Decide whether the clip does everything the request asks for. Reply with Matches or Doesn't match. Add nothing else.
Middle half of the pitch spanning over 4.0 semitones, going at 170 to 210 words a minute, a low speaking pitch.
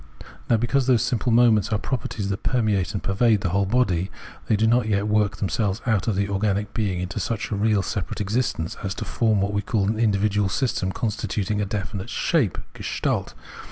Doesn't match